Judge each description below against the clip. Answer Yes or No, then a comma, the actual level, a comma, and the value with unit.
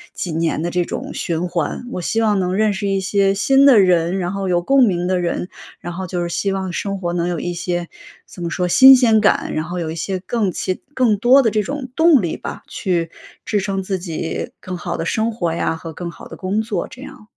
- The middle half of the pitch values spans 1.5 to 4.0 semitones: Yes, average, 3.4 semitones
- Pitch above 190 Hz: No, medium, 185 Hz